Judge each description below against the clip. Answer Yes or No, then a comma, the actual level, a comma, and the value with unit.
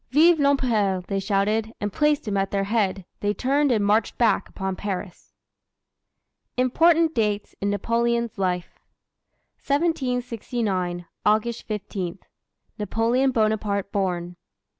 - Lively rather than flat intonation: No, average, 4.1 semitones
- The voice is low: No, high, 215 Hz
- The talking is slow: Yes, slow, 115 wpm